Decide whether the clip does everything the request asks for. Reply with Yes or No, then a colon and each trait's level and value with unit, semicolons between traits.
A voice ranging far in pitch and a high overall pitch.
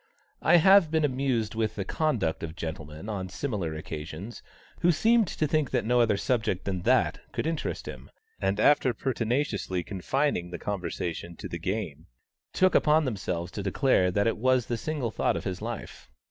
No: wide, 7.1 semitones; low, 110 Hz